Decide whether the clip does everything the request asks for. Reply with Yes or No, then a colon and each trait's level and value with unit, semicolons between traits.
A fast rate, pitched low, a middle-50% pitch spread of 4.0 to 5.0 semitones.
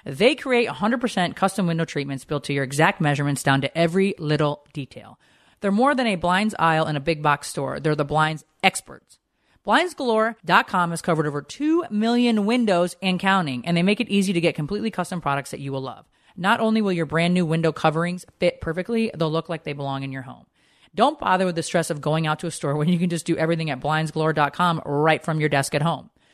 No: fast, 220 wpm; medium, 165 Hz; average, 4.3 semitones